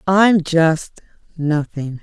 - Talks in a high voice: No, medium, 165 Hz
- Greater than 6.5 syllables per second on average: No, 2.8 syllables/s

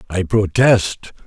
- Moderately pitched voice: No, low, 100 Hz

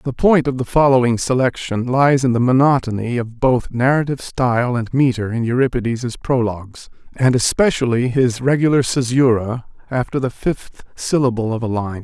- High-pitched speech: No, low, 125 Hz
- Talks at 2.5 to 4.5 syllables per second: No, 5.1 syllables/s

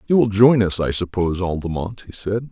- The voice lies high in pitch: No, low, 100 Hz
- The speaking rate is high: Yes, fast, 215 wpm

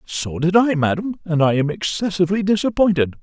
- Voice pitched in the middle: Yes, medium, 175 Hz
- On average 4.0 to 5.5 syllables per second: No, 5.7 syllables/s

